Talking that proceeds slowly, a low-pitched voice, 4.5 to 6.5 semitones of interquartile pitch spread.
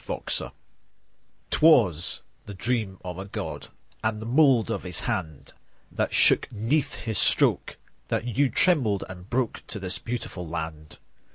No: average, 150 wpm; low, 105 Hz; average, 5.1 semitones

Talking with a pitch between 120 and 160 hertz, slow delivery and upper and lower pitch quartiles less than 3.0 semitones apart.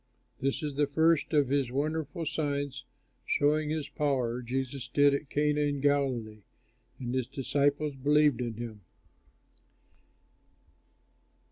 Yes: medium, 140 Hz; slow, 115 wpm; narrow, 2.4 semitones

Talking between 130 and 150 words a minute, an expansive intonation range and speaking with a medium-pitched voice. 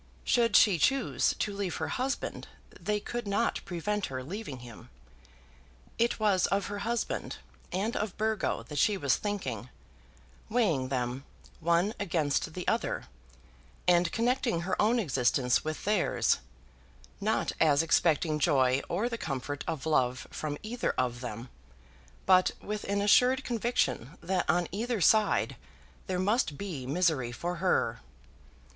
Yes: average, 140 wpm; wide, 6.7 semitones; medium, 180 Hz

